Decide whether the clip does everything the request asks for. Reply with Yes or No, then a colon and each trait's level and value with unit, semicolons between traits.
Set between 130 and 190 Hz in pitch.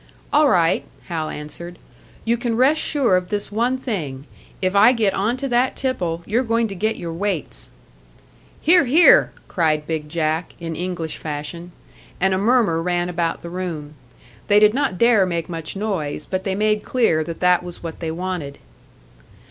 Yes: medium, 185 Hz